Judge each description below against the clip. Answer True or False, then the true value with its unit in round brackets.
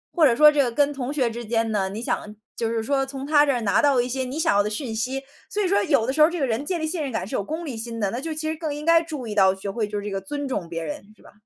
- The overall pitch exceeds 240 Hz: True (260 Hz)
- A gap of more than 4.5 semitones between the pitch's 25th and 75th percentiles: True (5.1 semitones)